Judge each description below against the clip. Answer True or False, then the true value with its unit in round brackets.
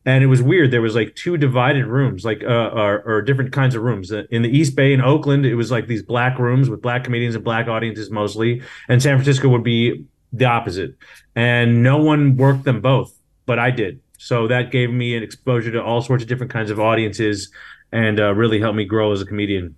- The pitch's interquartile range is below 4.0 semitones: True (2.8 semitones)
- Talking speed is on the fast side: True (230 wpm)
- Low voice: True (120 Hz)